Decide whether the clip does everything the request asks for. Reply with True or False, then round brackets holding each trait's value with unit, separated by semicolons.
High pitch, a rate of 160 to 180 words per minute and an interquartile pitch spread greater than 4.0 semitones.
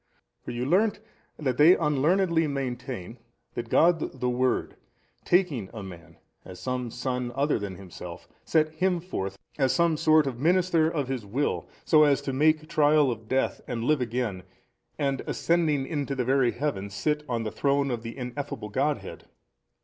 False (135 Hz; 165 wpm; 4.4 semitones)